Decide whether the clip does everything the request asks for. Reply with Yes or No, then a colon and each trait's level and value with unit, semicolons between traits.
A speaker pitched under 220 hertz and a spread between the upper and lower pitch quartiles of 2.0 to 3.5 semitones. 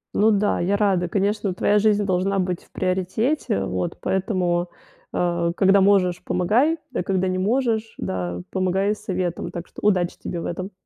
Yes: high, 190 Hz; narrow, 2.6 semitones